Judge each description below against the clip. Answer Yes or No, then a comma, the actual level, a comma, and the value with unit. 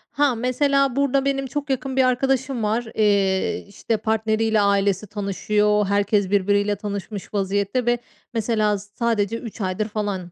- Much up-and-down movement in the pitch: No, average, 3.6 semitones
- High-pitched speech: Yes, high, 215 Hz